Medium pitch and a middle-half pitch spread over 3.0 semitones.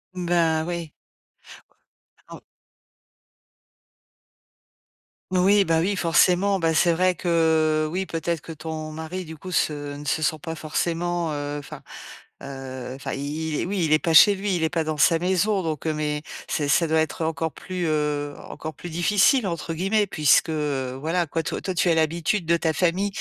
No: medium, 160 Hz; narrow, 2.4 semitones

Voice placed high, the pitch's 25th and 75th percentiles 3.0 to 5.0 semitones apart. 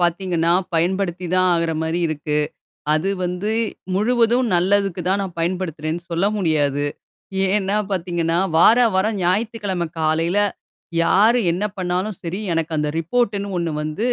No: medium, 180 Hz; average, 3.3 semitones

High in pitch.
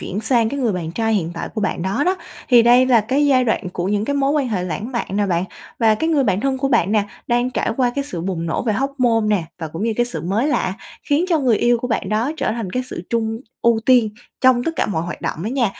Yes: high, 230 Hz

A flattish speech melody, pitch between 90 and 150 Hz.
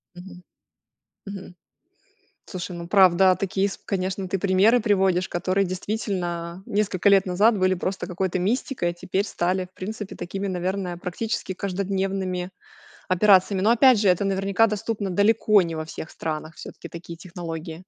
No: narrow, 2.0 semitones; high, 190 Hz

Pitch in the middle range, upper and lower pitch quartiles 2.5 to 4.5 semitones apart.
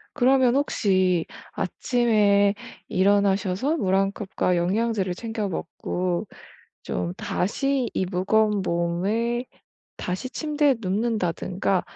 No: high, 200 Hz; average, 4.2 semitones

